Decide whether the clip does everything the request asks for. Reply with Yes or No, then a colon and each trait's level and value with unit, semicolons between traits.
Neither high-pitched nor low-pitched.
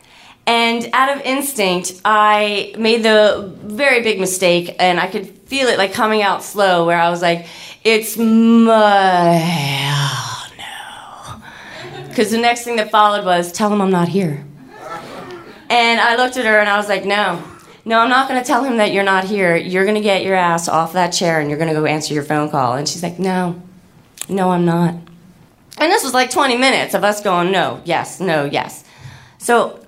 No: high, 195 Hz